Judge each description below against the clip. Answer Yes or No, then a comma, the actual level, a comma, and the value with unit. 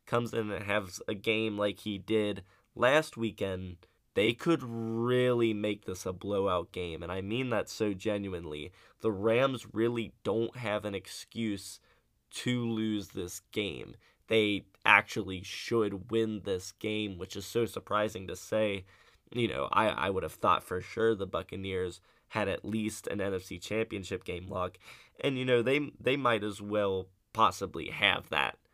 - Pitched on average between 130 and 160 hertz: No, low, 105 Hz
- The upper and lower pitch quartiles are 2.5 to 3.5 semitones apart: Yes, average, 2.9 semitones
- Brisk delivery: No, average, 165 wpm